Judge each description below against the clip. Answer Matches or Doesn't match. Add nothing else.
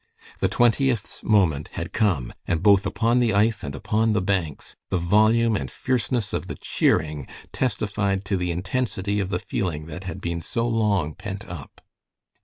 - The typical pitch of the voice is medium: Doesn't match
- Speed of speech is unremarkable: Matches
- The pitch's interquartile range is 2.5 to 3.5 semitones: Doesn't match